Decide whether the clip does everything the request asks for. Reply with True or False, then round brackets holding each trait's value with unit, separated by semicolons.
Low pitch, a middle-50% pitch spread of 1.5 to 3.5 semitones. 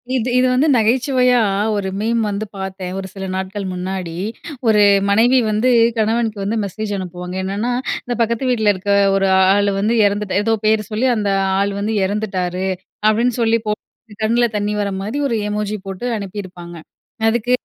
False (210 Hz; 2.9 semitones)